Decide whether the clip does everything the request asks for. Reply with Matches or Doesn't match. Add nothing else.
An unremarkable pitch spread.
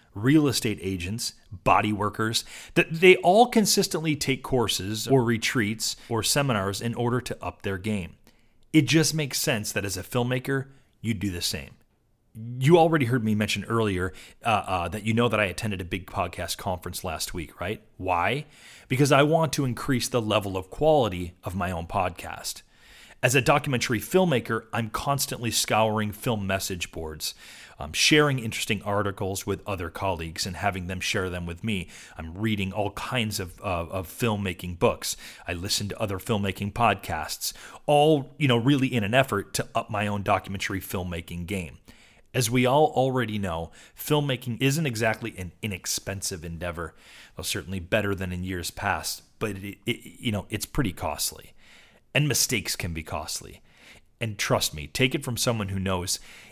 Matches